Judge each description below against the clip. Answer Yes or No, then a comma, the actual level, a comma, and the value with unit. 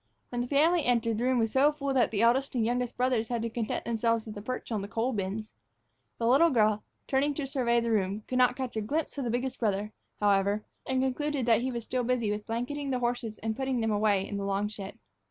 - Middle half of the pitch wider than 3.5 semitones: No, average, 3.2 semitones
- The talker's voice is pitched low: No, high, 235 Hz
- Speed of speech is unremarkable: No, fast, 255 wpm